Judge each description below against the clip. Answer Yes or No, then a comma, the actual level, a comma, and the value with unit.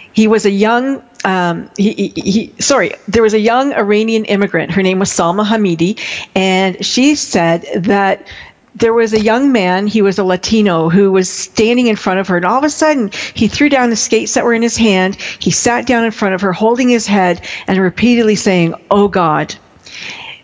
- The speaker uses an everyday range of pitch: Yes, average, 3.4 semitones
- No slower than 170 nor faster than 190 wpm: No, fast, 205 wpm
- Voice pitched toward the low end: No, high, 210 Hz